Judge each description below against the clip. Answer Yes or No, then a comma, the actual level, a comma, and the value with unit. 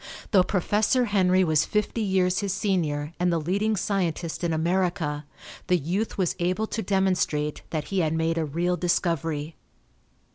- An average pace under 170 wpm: Yes, average, 155 wpm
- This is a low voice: No, medium, 180 Hz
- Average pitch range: Yes, average, 3.2 semitones